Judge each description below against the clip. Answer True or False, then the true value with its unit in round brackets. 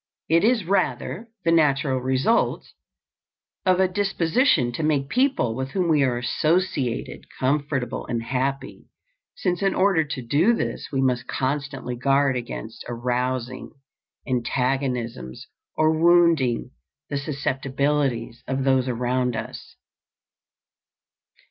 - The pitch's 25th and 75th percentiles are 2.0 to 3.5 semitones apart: False (4.4 semitones)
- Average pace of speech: False (115 wpm)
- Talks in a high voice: False (135 Hz)